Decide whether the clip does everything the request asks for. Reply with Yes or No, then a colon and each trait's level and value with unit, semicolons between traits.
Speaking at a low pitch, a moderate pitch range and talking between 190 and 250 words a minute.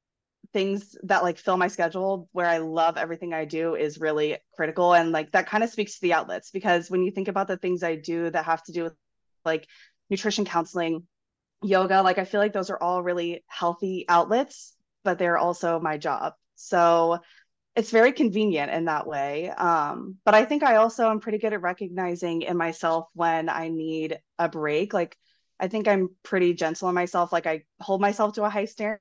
No: medium, 175 Hz; average, 3.2 semitones; fast, 205 wpm